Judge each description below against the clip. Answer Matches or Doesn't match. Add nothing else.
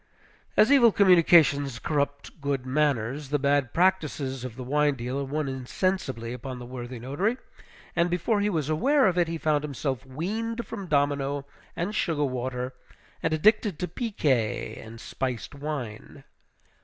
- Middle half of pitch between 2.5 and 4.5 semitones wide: Doesn't match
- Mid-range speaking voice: Matches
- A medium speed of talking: Matches